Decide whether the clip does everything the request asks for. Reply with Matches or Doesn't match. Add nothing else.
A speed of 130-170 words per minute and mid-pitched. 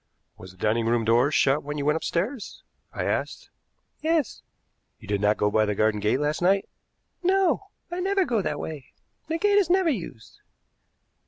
Doesn't match